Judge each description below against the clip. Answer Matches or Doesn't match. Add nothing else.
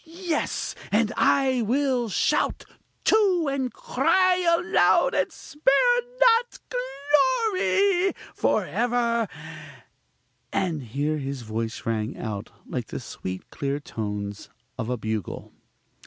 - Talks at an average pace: Doesn't match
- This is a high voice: Matches